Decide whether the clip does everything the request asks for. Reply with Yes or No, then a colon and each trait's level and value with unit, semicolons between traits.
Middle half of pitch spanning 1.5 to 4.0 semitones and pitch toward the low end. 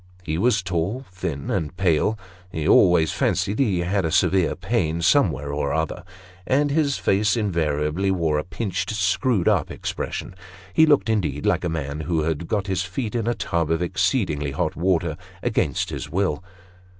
No: average, 4.4 semitones; very low, 90 Hz